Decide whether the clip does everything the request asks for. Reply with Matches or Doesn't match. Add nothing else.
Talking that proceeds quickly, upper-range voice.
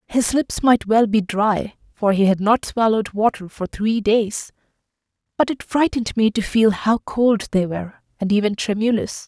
Doesn't match